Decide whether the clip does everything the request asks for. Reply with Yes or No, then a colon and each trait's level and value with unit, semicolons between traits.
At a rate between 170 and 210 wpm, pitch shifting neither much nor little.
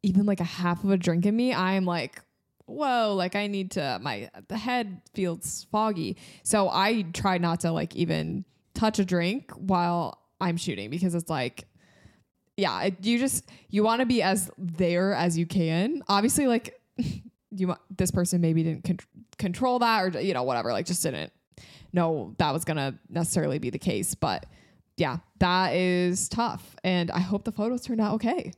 Yes: average, 185 wpm; average, 3.3 semitones